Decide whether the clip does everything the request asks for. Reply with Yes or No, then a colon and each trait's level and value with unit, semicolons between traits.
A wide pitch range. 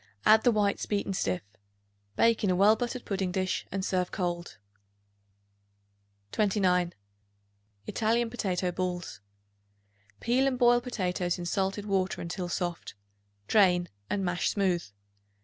No: average, 3.2 semitones